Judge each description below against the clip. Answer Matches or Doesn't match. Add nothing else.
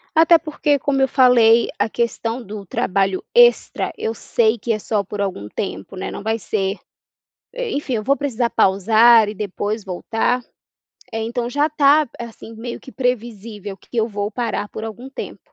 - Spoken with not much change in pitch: Doesn't match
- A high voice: Matches